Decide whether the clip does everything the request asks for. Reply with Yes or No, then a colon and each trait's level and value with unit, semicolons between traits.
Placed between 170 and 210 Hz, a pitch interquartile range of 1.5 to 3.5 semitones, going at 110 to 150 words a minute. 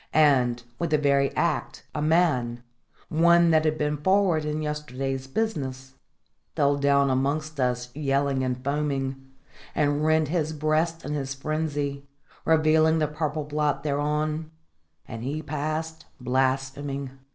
No: medium, 145 Hz; narrow, 2.4 semitones; slow, 135 wpm